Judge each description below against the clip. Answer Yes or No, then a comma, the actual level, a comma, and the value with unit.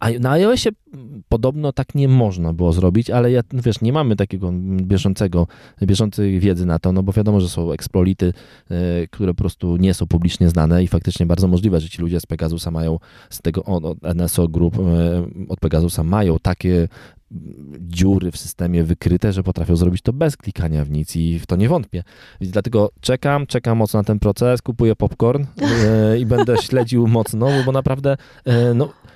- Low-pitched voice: Yes, very low, 95 Hz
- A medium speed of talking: No, fast, 175 wpm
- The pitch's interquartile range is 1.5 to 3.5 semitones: No, average, 5.3 semitones